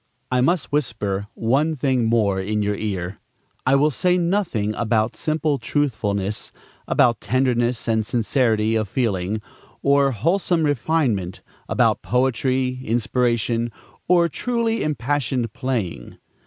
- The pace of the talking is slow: Yes, slow, 115 wpm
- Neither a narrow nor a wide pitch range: Yes, average, 4.9 semitones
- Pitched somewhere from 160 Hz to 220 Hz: No, low, 120 Hz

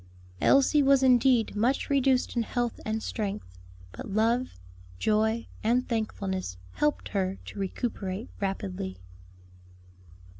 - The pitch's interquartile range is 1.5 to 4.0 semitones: No, average, 4.4 semitones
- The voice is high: Yes, high, 220 Hz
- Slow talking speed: Yes, slow, 110 wpm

